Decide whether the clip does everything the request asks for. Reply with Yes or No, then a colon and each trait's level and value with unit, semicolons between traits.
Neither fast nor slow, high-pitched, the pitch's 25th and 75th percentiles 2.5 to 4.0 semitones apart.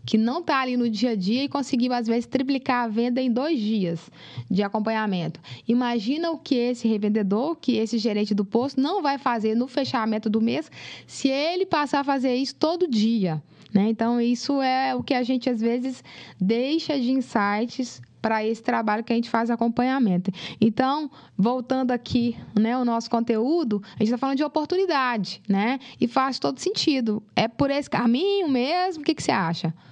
No: fast, 190 wpm; high, 240 Hz; average, 3.6 semitones